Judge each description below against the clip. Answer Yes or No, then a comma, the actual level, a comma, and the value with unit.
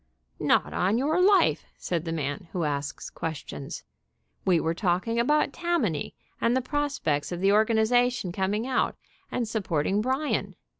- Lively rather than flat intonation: Yes, wide, 7.0 semitones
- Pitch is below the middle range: No, high, 210 Hz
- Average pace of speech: Yes, average, 155 wpm